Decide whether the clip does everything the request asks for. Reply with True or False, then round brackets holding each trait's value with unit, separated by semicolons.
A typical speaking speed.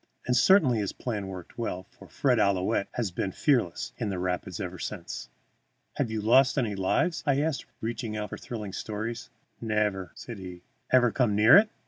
True (180 wpm)